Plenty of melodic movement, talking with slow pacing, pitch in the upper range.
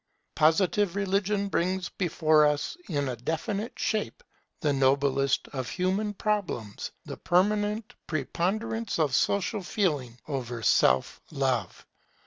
No: wide, 6.7 semitones; slow, 115 wpm; medium, 170 Hz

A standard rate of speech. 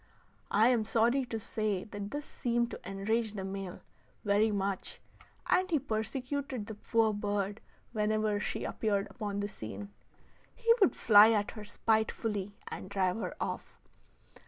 Yes: average, 150 wpm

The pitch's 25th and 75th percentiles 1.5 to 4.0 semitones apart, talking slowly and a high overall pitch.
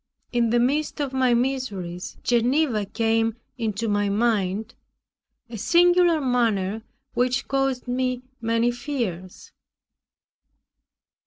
Yes: average, 3.2 semitones; slow, 100 wpm; high, 240 Hz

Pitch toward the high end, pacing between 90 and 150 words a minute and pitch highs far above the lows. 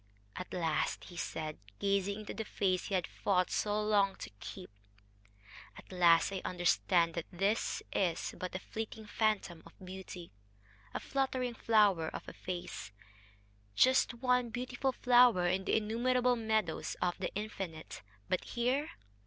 No: high, 200 Hz; average, 145 wpm; average, 4.3 semitones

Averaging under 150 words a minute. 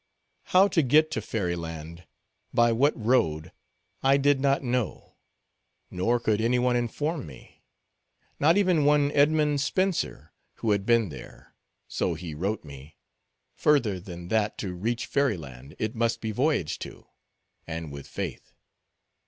Yes: average, 140 wpm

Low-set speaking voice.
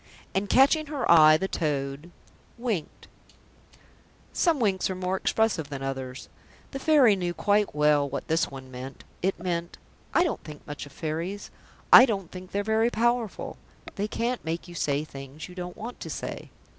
No: medium, 180 Hz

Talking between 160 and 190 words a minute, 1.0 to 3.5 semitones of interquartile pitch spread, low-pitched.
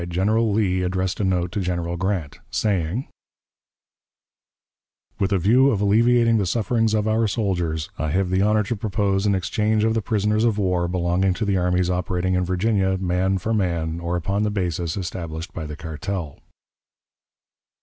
Yes: average, 170 wpm; average, 3.2 semitones; very low, 95 Hz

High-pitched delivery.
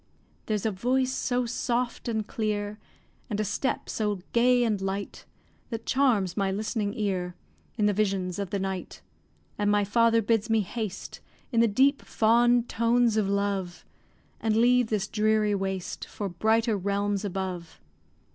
Yes: high, 210 Hz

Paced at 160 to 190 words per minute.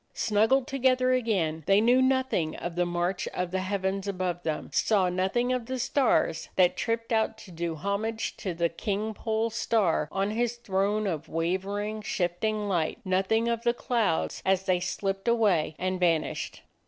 Yes: average, 170 wpm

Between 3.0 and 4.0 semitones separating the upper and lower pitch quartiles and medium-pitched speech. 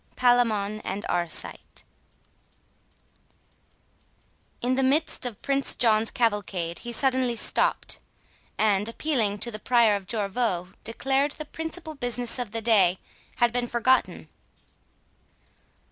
No: average, 3.7 semitones; high, 235 Hz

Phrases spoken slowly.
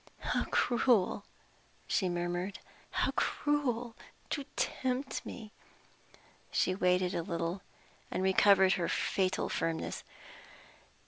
Yes: slow, 95 wpm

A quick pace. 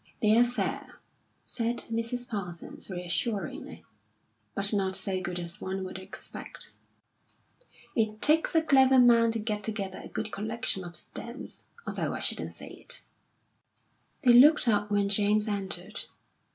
No: average, 140 wpm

